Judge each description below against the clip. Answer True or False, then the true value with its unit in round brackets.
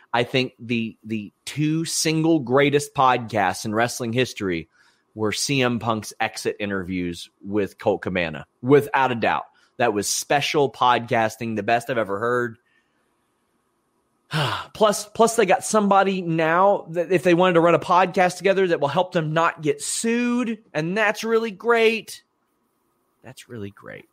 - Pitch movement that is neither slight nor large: False (8.0 semitones)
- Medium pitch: True (145 Hz)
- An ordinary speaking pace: True (150 wpm)